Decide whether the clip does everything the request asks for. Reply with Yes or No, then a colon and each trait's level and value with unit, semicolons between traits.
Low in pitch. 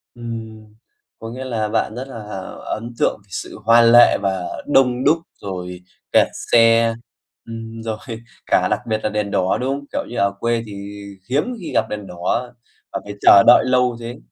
Yes: low, 115 Hz